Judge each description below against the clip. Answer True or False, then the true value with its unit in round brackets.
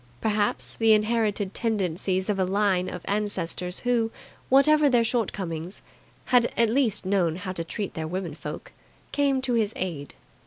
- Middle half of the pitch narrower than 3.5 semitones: False (3.9 semitones)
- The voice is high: True (205 Hz)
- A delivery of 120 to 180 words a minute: True (155 wpm)